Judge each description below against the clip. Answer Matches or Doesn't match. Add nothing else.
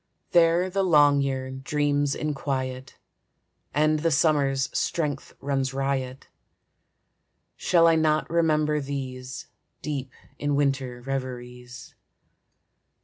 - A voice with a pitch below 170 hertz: Matches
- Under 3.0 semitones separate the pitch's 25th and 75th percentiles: Matches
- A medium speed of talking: Doesn't match